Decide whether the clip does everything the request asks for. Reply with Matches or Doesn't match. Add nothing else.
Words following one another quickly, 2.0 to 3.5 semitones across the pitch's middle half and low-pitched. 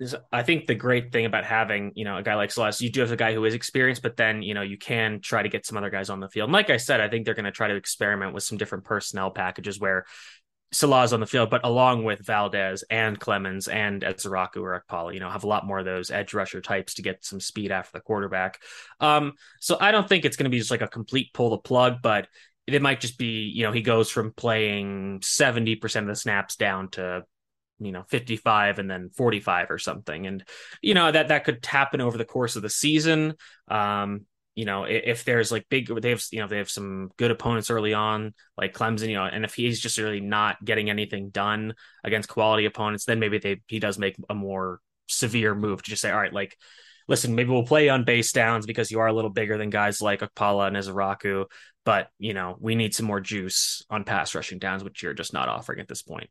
Matches